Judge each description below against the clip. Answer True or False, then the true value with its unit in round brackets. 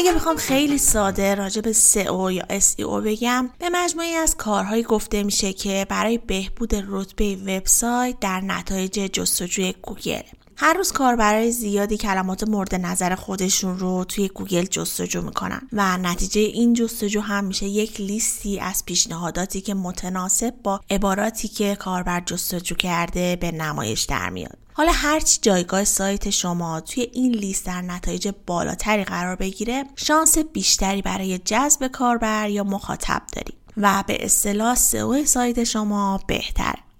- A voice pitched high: True (200 Hz)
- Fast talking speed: False (145 wpm)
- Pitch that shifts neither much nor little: True (3.4 semitones)